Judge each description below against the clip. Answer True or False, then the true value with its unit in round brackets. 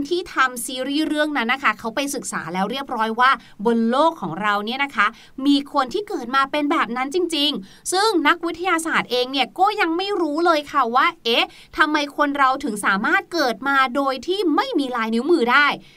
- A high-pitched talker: True (280 Hz)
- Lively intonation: False (4.8 semitones)